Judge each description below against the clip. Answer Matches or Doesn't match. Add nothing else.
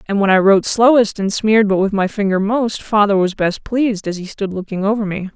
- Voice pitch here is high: Matches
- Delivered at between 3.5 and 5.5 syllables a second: Doesn't match